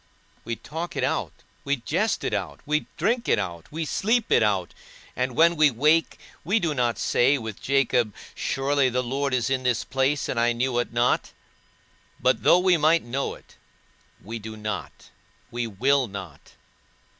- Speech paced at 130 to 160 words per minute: No, average, 175 wpm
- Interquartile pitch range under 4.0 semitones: No, average, 4.6 semitones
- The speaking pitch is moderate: No, low, 130 Hz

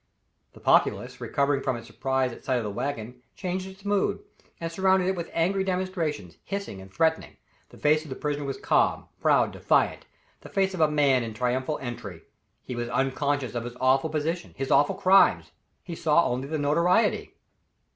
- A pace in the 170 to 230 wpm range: Yes, average, 185 wpm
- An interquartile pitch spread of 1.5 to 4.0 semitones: No, wide, 5.6 semitones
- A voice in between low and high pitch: Yes, medium, 145 Hz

